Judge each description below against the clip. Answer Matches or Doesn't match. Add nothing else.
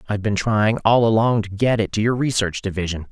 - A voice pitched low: Matches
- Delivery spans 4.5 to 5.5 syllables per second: Doesn't match